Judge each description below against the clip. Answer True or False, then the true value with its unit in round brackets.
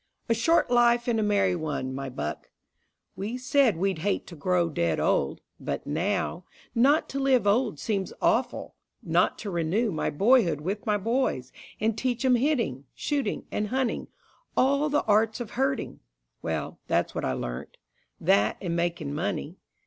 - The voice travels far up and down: True (6.5 semitones)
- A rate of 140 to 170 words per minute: True (165 wpm)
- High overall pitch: True (205 Hz)